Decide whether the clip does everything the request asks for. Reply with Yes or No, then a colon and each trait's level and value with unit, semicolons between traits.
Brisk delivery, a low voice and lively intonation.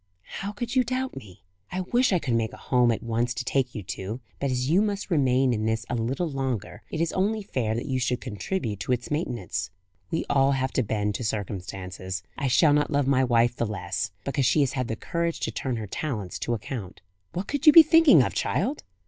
Yes: fast, 230 wpm; low, 130 Hz; wide, 6.5 semitones